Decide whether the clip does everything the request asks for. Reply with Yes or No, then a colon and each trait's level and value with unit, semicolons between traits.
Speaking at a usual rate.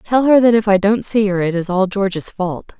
No: fast, 280 wpm